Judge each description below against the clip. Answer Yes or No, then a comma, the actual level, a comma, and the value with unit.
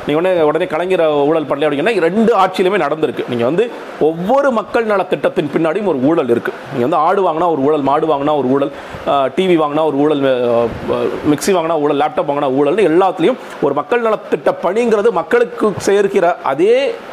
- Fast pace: Yes, fast, 170 wpm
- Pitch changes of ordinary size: No, wide, 8.2 semitones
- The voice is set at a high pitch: No, medium, 180 Hz